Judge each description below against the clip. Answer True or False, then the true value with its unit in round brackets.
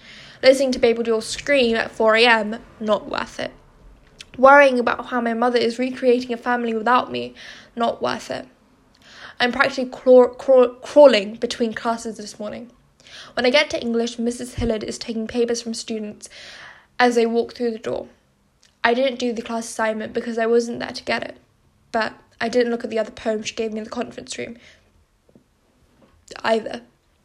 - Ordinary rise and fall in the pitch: False (1.5 semitones)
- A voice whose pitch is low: False (235 Hz)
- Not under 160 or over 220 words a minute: True (175 wpm)